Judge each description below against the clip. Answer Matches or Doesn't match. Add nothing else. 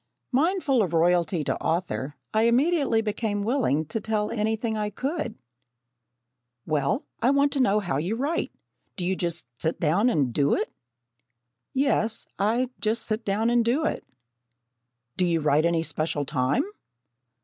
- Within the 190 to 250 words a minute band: Doesn't match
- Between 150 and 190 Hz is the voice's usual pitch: Doesn't match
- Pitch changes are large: Matches